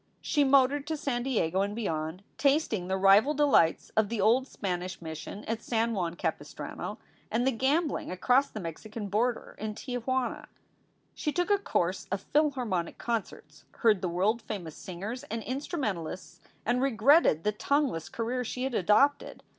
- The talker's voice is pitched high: Yes, high, 225 Hz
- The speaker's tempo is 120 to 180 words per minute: Yes, average, 160 wpm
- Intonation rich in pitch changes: Yes, wide, 5.9 semitones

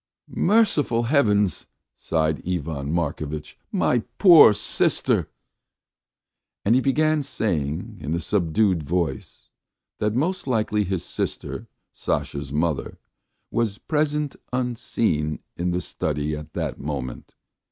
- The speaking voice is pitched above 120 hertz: No, very low, 95 Hz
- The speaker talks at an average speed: No, slow, 110 wpm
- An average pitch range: No, wide, 8.4 semitones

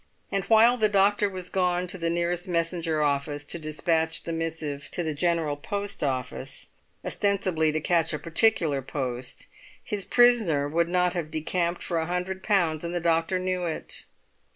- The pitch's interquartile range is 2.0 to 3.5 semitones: Yes, average, 2.9 semitones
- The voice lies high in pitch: No, medium, 170 Hz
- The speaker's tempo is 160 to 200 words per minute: Yes, average, 170 wpm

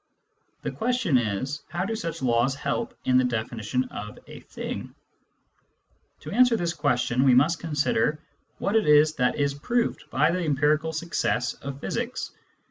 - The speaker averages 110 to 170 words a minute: Yes, average, 165 wpm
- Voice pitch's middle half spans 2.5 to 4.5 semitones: No, average, 5.2 semitones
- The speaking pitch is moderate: Yes, medium, 150 Hz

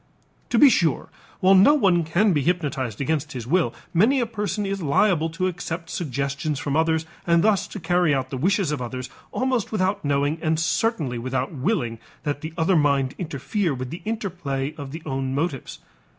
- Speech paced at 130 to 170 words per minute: No, average, 185 wpm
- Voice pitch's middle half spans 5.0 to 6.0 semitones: Yes, average, 5.3 semitones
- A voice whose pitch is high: No, medium, 160 Hz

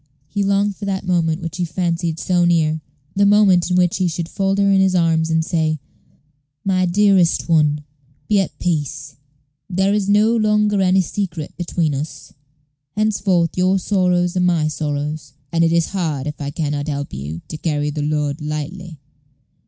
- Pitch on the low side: No, medium, 175 Hz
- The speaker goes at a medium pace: Yes, average, 175 wpm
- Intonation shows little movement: No, average, 3.8 semitones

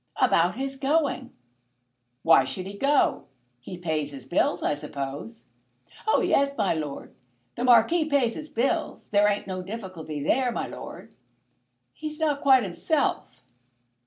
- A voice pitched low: No, high, 225 Hz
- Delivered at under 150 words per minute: Yes, average, 140 wpm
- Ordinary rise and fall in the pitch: No, wide, 8.8 semitones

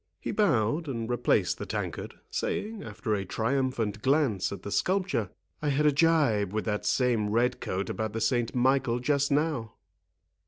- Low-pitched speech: Yes, low, 125 Hz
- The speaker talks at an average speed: Yes, average, 165 wpm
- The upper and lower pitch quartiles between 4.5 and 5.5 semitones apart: Yes, average, 4.9 semitones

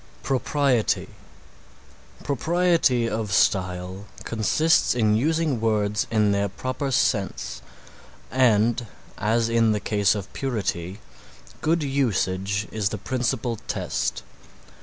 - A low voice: Yes, low, 110 Hz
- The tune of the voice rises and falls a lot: No, average, 4.2 semitones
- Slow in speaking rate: Yes, slow, 100 wpm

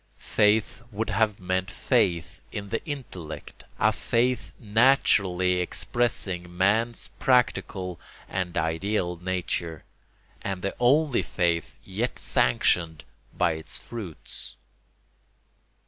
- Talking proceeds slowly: Yes, slow, 100 wpm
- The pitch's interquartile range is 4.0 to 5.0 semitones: Yes, average, 4.4 semitones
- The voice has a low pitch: Yes, very low, 95 Hz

